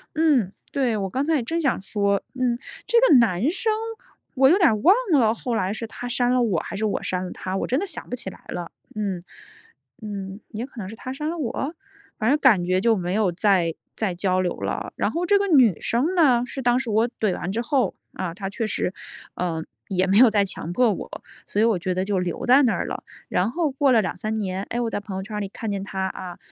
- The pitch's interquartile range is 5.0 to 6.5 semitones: Yes, average, 5.3 semitones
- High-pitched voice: Yes, high, 220 Hz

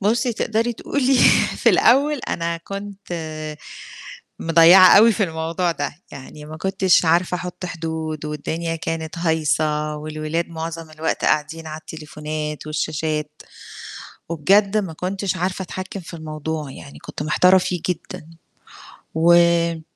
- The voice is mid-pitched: Yes, medium, 165 Hz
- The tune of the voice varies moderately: Yes, average, 3.0 semitones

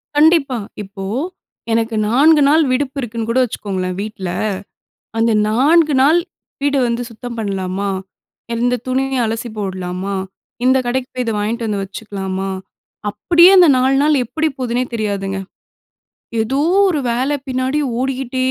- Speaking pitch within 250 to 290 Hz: No, high, 240 Hz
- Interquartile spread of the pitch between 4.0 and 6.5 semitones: Yes, average, 4.4 semitones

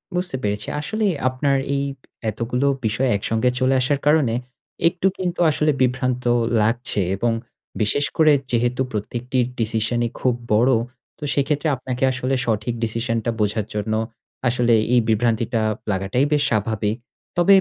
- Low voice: Yes, low, 125 Hz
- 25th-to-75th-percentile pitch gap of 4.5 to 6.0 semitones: No, average, 3.5 semitones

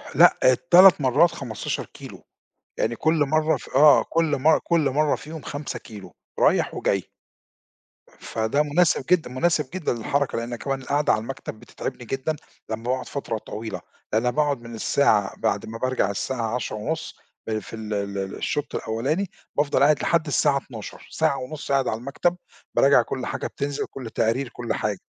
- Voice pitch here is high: No, low, 135 Hz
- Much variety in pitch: No, average, 4.8 semitones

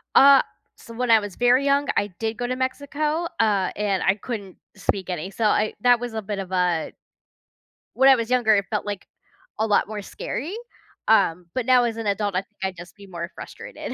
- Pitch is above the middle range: Yes, high, 215 Hz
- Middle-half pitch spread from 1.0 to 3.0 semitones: No, average, 4.3 semitones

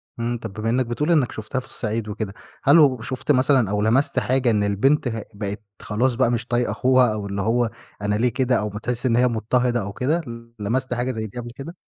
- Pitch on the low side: Yes, low, 120 Hz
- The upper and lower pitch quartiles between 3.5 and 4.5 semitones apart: No, average, 3.1 semitones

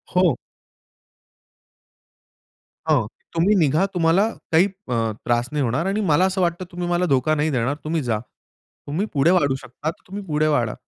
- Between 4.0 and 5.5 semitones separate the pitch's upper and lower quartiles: Yes, average, 4.7 semitones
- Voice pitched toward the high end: No, medium, 160 Hz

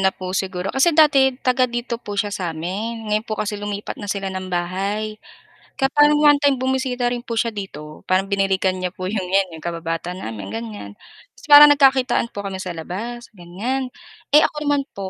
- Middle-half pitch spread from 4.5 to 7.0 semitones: Yes, average, 5.2 semitones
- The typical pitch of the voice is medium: No, high, 205 Hz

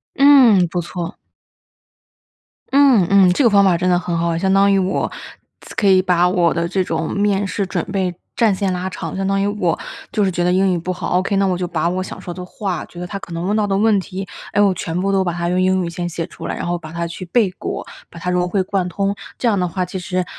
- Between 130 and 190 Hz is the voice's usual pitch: Yes, medium, 185 Hz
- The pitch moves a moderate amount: No, narrow, 2.0 semitones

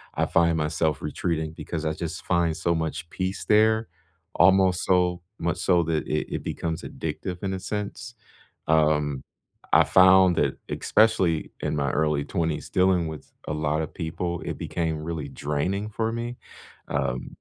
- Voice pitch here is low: Yes, very low, 85 Hz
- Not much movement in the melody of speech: No, average, 3.2 semitones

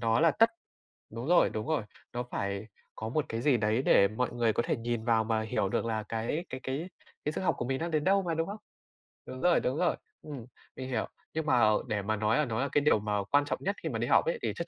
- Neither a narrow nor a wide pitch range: No, wide, 5.8 semitones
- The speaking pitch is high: No, low, 125 Hz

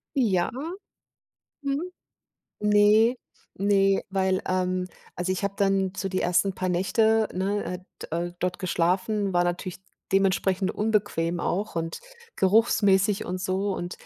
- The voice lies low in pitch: No, high, 190 Hz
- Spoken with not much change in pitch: Yes, narrow, 2.1 semitones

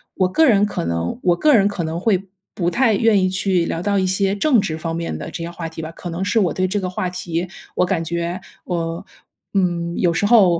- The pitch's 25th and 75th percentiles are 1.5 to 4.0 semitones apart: Yes, average, 2.8 semitones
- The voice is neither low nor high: Yes, medium, 180 Hz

